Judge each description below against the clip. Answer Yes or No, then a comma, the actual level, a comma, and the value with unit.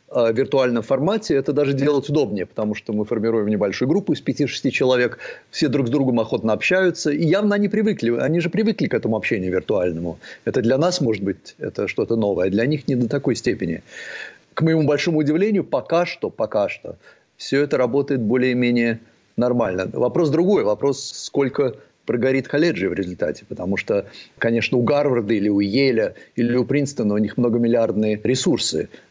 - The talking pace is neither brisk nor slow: No, fast, 170 wpm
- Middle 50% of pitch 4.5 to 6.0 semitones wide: Yes, average, 4.9 semitones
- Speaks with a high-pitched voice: No, low, 130 Hz